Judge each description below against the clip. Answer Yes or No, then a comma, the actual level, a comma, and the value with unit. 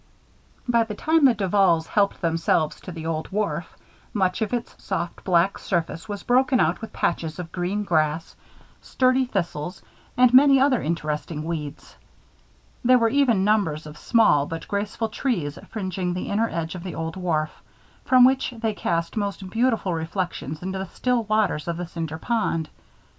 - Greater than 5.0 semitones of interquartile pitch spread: Yes, wide, 5.5 semitones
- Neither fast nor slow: Yes, average, 165 wpm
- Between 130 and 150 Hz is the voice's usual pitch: No, high, 190 Hz